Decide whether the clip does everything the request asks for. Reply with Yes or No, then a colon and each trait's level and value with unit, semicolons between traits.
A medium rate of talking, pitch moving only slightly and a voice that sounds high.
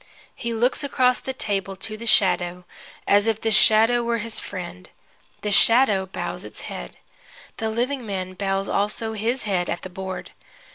No: average, 170 wpm; average, 3.6 semitones; high, 210 Hz